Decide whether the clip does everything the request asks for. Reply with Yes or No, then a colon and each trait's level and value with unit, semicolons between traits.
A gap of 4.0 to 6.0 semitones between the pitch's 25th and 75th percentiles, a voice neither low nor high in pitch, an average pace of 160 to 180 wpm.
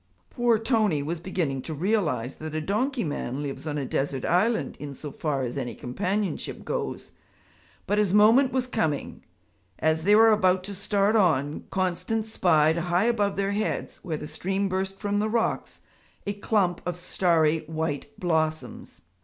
Yes: average, 5.1 semitones; medium, 180 Hz; average, 165 wpm